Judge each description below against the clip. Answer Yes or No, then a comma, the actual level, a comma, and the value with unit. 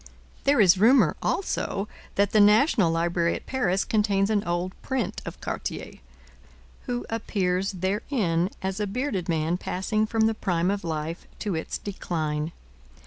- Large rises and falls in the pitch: No, average, 3.9 semitones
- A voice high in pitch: Yes, high, 195 Hz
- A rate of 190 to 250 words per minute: No, average, 145 wpm